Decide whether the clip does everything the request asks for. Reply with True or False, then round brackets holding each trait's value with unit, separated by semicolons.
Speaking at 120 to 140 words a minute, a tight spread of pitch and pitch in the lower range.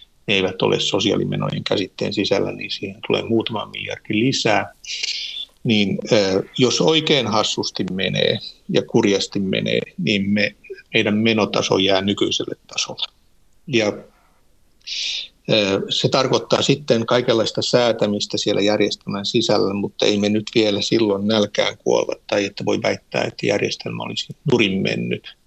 True (125 wpm; 1.8 semitones; 105 Hz)